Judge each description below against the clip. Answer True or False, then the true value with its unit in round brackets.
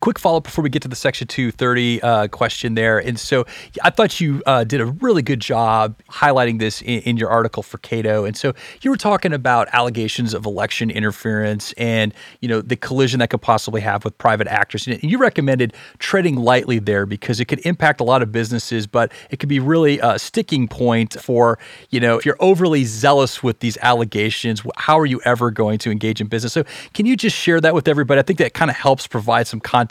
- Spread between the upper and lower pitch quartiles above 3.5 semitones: True (4.1 semitones)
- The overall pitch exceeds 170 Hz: False (120 Hz)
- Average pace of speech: False (225 wpm)